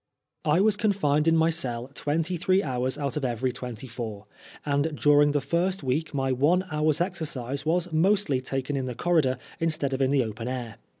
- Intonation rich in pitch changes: No, average, 4.2 semitones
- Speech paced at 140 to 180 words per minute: No, average, 190 wpm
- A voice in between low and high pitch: Yes, medium, 145 Hz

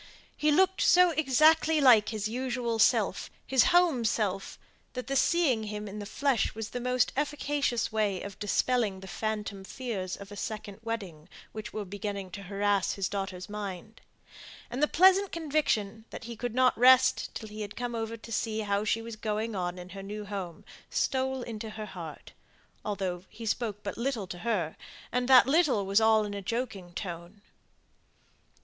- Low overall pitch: No, high, 220 Hz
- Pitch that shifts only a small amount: No, average, 4.0 semitones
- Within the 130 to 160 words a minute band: No, average, 180 wpm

